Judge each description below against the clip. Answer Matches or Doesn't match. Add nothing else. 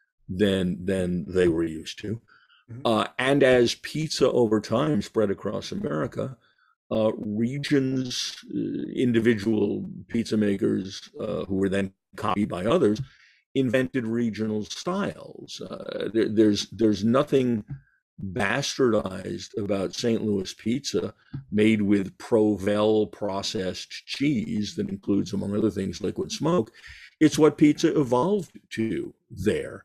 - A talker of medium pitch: Doesn't match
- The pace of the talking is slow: Matches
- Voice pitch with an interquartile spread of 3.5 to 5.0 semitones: Matches